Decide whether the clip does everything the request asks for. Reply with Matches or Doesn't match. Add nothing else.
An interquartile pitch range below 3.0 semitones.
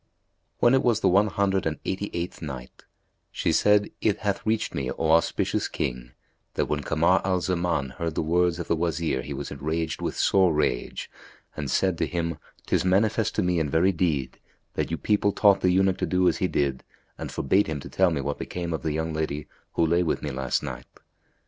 Doesn't match